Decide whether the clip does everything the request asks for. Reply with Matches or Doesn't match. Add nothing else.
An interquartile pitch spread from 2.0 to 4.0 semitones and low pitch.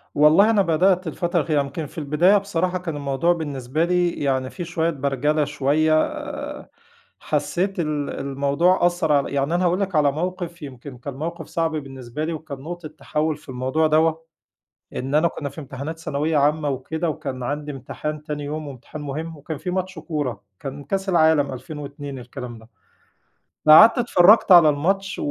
Doesn't match